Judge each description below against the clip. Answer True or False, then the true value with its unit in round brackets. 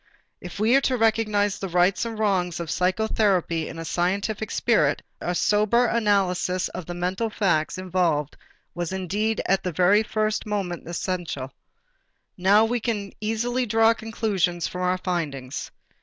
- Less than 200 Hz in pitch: True (190 Hz)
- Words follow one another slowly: False (155 wpm)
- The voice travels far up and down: False (3.6 semitones)